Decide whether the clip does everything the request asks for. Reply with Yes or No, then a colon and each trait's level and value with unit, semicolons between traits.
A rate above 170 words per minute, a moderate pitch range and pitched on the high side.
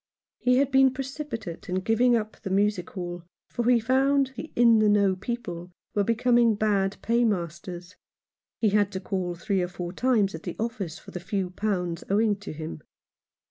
Yes: average, 180 wpm; average, 4.6 semitones; high, 205 Hz